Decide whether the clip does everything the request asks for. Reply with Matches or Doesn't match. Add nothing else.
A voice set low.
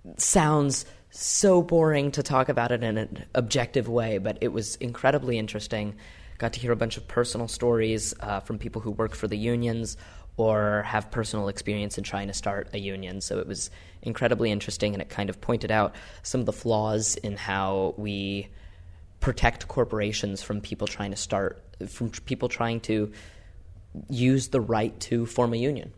Matches